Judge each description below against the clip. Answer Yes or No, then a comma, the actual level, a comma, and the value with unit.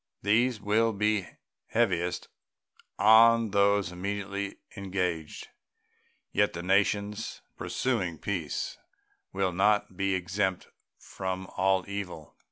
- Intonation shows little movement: Yes, narrow, 2.1 semitones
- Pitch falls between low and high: No, low, 100 Hz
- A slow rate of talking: Yes, slow, 95 wpm